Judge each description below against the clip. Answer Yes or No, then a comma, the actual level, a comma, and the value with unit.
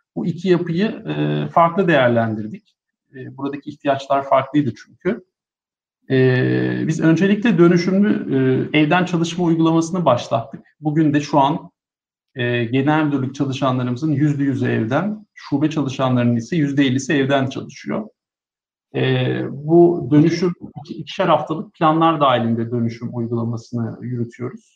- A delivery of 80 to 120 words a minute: Yes, average, 105 wpm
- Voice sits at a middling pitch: Yes, medium, 145 Hz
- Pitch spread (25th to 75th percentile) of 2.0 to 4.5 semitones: No, average, 5.3 semitones